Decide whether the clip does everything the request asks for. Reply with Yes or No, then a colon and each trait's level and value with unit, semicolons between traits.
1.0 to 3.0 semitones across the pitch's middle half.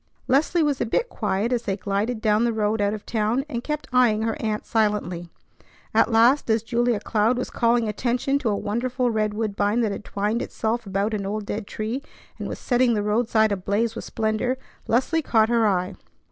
Yes: narrow, 2.5 semitones